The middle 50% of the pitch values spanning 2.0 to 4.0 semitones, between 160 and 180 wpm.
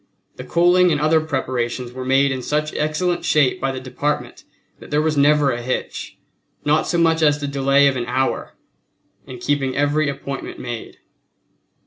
Yes: average, 2.8 semitones; average, 170 wpm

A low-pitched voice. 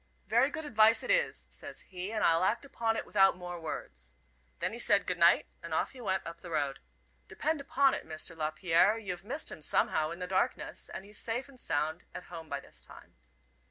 No: medium, 185 Hz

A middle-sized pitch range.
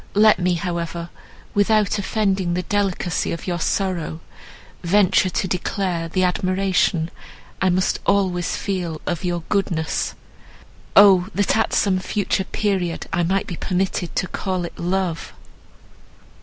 No: narrow, 2.2 semitones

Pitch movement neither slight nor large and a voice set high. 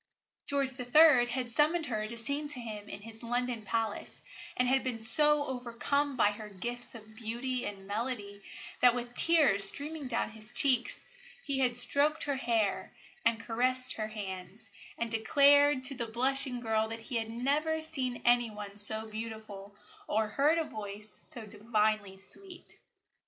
Yes: average, 3.7 semitones; high, 235 Hz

